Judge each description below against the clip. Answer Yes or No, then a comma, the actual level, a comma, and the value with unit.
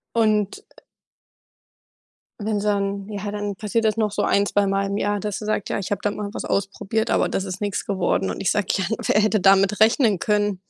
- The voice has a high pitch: Yes, high, 205 Hz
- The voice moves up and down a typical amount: No, narrow, 1.2 semitones